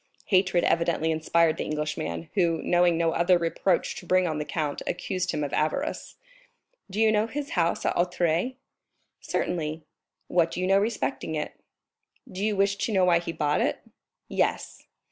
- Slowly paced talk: No, average, 170 wpm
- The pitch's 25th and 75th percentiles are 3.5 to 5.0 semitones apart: No, average, 3.1 semitones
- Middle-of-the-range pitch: Yes, medium, 170 Hz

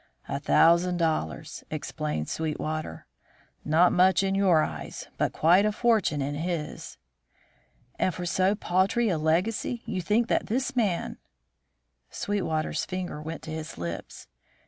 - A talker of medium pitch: Yes, medium, 175 Hz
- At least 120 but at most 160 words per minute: Yes, average, 140 wpm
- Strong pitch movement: No, average, 3.9 semitones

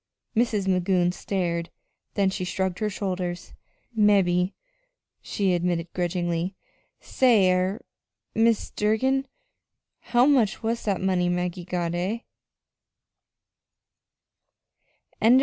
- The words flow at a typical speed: No, slow, 95 wpm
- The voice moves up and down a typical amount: Yes, average, 3.1 semitones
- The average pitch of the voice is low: No, high, 190 Hz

